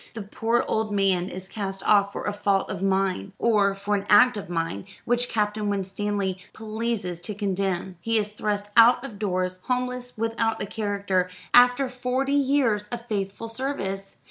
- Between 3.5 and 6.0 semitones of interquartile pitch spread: No, average, 2.9 semitones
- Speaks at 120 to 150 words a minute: No, average, 170 wpm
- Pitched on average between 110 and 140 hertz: No, high, 205 Hz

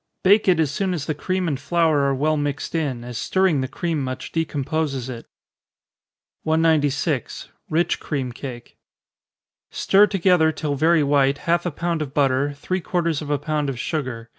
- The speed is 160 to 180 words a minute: Yes, average, 170 wpm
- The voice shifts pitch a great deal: No, average, 3.4 semitones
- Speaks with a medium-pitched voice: Yes, medium, 150 Hz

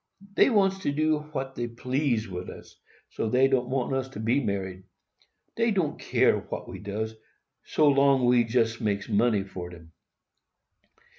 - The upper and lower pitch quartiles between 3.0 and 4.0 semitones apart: No, average, 4.7 semitones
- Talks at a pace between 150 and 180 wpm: Yes, average, 160 wpm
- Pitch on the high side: No, low, 125 Hz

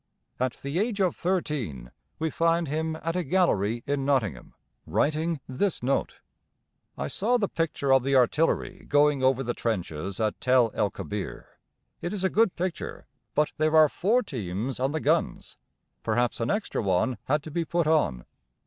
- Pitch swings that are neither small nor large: No, wide, 5.9 semitones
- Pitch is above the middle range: No, medium, 145 Hz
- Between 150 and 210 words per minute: Yes, average, 170 wpm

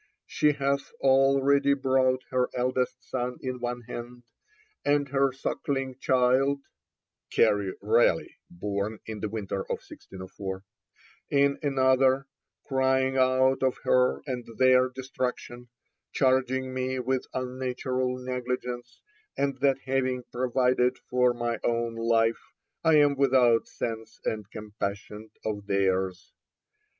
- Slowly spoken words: Yes, slow, 115 wpm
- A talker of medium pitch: No, low, 125 Hz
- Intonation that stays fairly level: Yes, narrow, 2.0 semitones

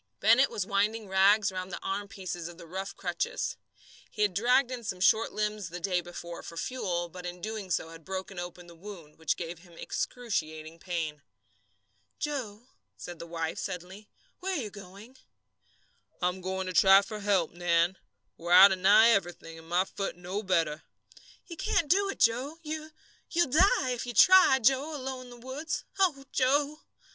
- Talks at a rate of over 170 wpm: Yes, average, 180 wpm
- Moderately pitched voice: No, high, 195 Hz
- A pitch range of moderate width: No, wide, 5.9 semitones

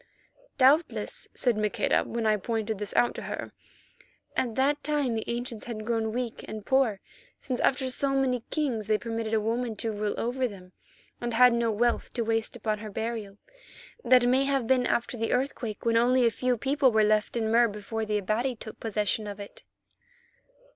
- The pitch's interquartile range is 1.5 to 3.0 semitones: Yes, average, 2.7 semitones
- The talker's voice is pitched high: Yes, high, 230 Hz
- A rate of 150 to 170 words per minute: No, average, 190 wpm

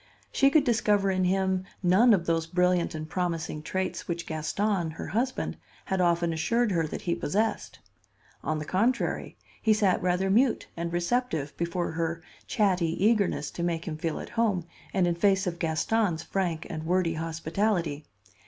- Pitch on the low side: No, medium, 180 Hz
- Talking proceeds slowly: No, average, 165 wpm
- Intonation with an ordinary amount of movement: Yes, average, 3.4 semitones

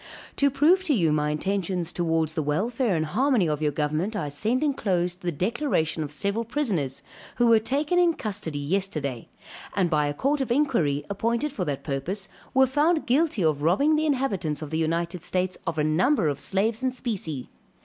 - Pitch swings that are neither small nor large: No, wide, 8.5 semitones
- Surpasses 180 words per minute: Yes, average, 190 wpm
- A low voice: No, high, 190 Hz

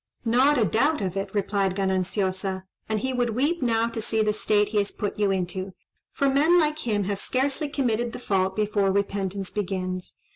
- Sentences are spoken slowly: No, average, 190 wpm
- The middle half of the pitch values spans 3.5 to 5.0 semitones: Yes, average, 4.1 semitones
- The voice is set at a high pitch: Yes, high, 210 Hz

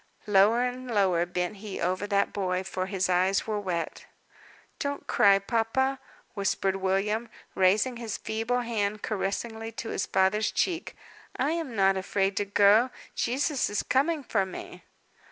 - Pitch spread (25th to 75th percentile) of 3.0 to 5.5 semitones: Yes, average, 3.5 semitones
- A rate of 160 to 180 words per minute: No, average, 150 wpm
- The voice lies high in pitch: Yes, high, 205 Hz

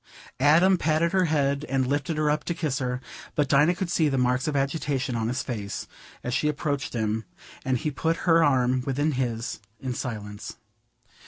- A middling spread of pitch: Yes, average, 3.5 semitones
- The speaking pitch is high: No, medium, 140 Hz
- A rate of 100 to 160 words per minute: No, average, 185 wpm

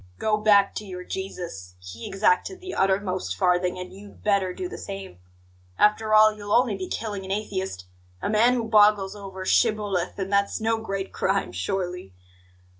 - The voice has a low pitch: No, high, 195 Hz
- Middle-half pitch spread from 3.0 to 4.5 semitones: No, narrow, 2.6 semitones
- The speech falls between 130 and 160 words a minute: No, average, 170 wpm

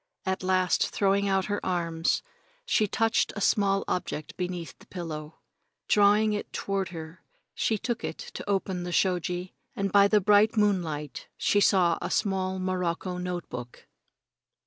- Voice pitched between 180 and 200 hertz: Yes, medium, 185 Hz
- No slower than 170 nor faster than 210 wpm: No, average, 150 wpm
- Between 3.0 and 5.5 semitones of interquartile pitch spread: No, narrow, 2.4 semitones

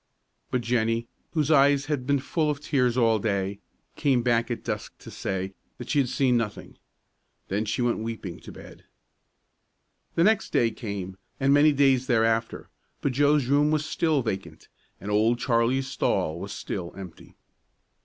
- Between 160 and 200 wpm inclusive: Yes, average, 165 wpm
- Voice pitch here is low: Yes, low, 120 Hz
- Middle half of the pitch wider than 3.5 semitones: Yes, average, 4.4 semitones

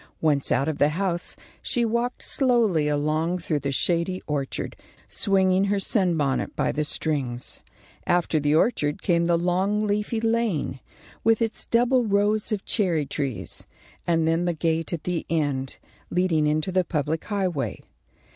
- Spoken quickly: No, average, 150 wpm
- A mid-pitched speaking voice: Yes, medium, 170 Hz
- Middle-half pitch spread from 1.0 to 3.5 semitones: No, average, 5.1 semitones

